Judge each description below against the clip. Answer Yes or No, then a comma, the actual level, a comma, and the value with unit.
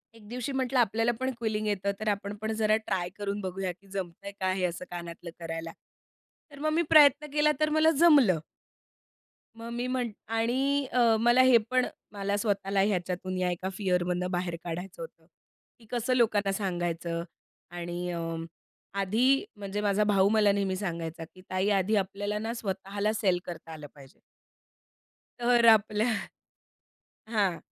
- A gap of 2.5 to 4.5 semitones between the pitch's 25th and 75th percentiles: Yes, average, 4.2 semitones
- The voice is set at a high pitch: Yes, high, 200 Hz